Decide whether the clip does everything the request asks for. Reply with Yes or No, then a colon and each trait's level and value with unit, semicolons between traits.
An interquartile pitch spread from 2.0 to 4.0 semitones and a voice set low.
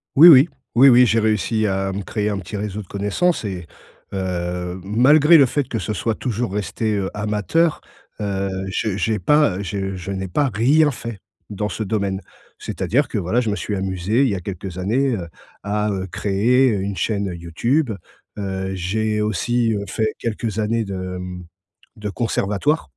Yes: average, 3.4 semitones; low, 105 Hz